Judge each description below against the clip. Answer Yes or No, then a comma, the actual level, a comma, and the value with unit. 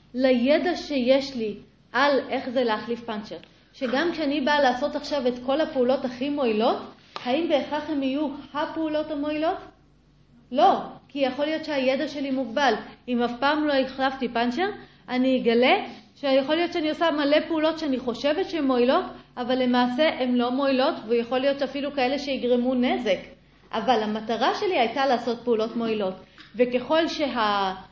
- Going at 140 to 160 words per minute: Yes, fast, 150 wpm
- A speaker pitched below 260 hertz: No, very high, 265 Hz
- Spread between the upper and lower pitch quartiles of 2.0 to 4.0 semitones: Yes, average, 3.3 semitones